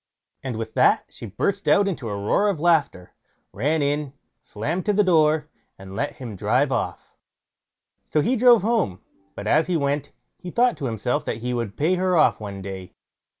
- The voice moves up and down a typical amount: No, wide, 8.5 semitones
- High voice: No, medium, 145 Hz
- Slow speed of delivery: No, average, 190 wpm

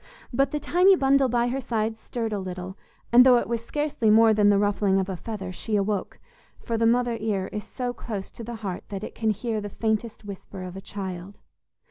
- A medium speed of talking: No, fast, 220 wpm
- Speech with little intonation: No, average, 3.2 semitones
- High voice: Yes, high, 220 Hz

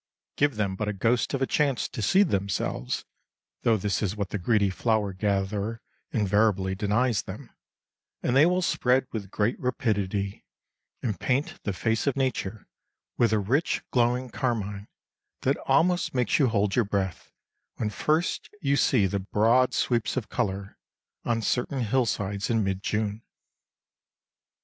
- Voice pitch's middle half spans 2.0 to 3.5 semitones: No, average, 4.1 semitones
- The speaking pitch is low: Yes, low, 110 Hz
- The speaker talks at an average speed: Yes, average, 150 wpm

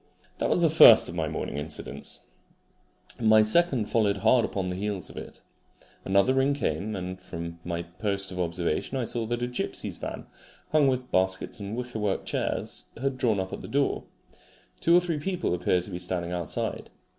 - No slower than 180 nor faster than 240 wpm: Yes, average, 185 wpm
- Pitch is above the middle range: No, low, 105 Hz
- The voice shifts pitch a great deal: Yes, wide, 5.7 semitones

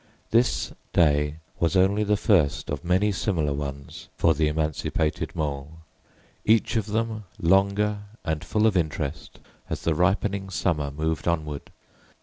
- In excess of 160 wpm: No, slow, 135 wpm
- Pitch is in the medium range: No, very low, 85 Hz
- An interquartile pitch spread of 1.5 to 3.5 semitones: No, average, 5.1 semitones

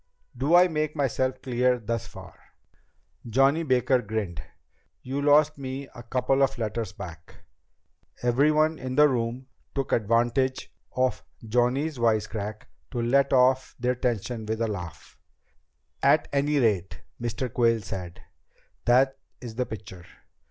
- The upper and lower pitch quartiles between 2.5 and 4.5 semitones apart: Yes, average, 3.3 semitones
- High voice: No, low, 125 Hz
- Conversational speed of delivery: No, slow, 130 wpm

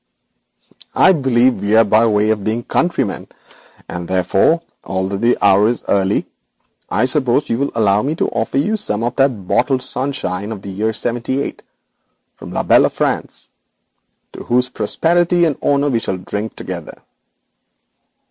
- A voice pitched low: Yes, low, 115 Hz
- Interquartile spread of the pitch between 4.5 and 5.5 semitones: Yes, average, 5.1 semitones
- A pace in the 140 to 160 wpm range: Yes, average, 155 wpm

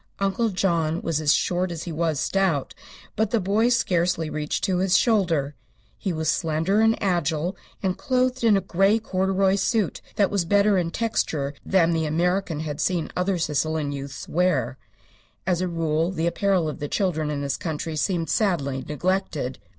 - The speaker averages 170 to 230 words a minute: Yes, average, 175 wpm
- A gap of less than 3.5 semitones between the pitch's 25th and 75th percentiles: No, average, 3.8 semitones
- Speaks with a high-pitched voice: No, medium, 175 Hz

